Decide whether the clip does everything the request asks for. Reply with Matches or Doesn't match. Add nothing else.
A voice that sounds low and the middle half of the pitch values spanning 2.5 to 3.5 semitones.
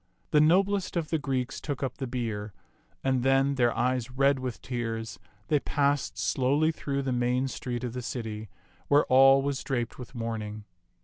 Matches